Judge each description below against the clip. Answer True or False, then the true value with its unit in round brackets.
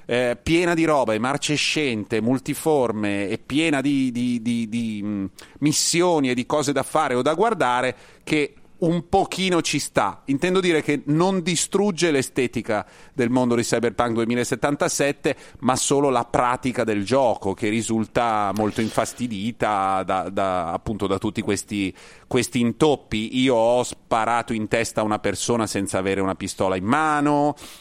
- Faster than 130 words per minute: True (150 wpm)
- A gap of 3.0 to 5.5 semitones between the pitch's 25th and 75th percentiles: True (5.1 semitones)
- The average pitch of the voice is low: True (125 Hz)